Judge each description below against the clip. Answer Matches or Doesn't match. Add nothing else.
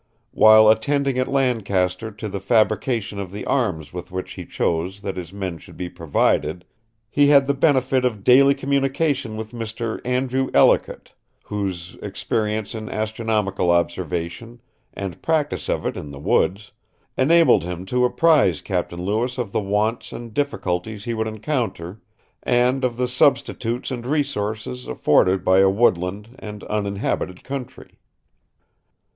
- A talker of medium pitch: Doesn't match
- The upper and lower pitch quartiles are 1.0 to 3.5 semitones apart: Doesn't match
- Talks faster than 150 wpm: Doesn't match